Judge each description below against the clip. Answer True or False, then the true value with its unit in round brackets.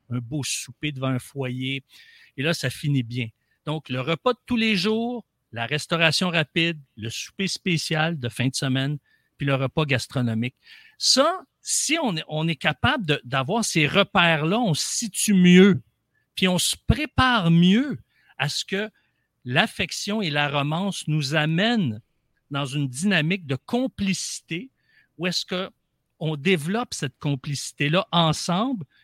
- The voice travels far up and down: True (6.3 semitones)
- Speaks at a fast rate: False (150 wpm)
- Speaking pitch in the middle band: True (160 Hz)